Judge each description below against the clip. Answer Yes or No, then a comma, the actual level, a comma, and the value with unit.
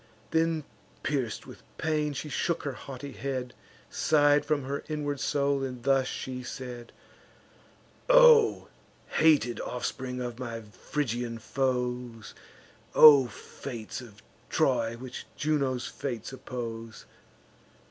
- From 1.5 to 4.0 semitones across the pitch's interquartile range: Yes, average, 3.1 semitones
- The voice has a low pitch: Yes, low, 130 Hz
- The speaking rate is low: Yes, slow, 110 wpm